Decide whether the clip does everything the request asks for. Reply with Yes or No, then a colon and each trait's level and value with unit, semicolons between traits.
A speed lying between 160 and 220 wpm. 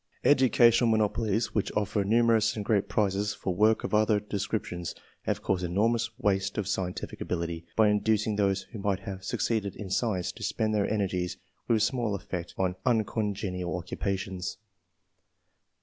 No: average, 150 wpm